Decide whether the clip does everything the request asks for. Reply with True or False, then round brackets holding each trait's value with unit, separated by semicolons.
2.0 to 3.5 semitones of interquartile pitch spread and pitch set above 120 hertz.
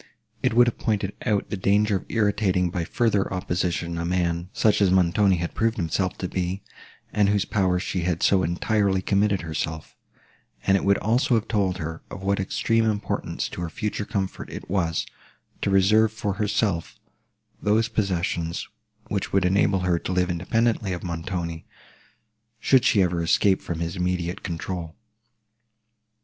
False (3.0 semitones; 95 Hz)